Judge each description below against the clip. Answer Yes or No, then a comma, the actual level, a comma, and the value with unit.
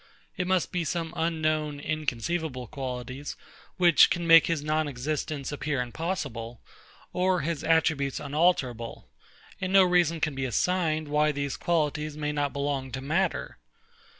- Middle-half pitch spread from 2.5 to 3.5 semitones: Yes, average, 3.1 semitones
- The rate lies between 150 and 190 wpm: No, average, 140 wpm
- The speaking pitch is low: No, medium, 150 Hz